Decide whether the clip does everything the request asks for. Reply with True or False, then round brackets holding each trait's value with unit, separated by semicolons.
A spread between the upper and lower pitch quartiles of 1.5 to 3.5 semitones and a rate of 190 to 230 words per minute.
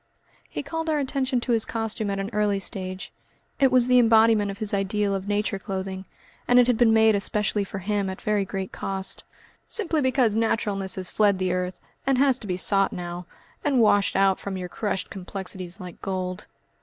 True (3.1 semitones; 195 wpm)